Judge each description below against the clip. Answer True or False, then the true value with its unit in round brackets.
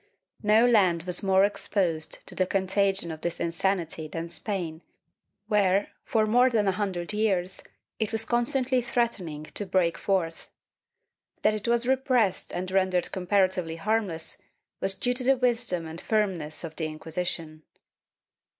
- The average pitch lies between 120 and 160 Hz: False (190 Hz)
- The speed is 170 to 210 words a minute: False (145 wpm)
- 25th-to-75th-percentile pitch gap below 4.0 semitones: False (4.4 semitones)